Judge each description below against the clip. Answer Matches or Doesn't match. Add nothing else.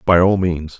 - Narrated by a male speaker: Matches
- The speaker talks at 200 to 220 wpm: Doesn't match